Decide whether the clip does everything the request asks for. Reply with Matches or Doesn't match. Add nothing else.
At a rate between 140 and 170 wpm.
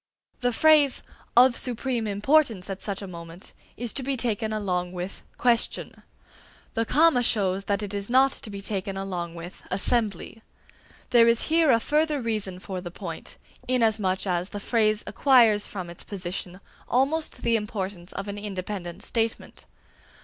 Matches